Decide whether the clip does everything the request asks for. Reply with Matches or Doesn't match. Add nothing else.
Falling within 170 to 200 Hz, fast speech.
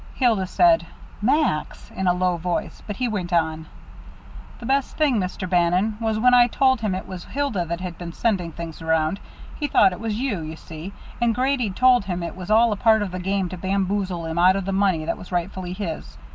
Matches